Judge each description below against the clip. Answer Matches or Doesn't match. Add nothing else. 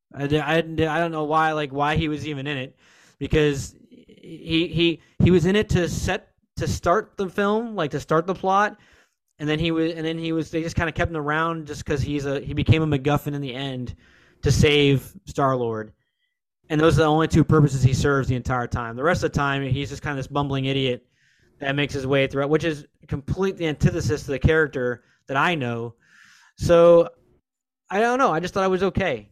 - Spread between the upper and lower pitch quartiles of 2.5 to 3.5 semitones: Matches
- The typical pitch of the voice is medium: Matches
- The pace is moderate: Doesn't match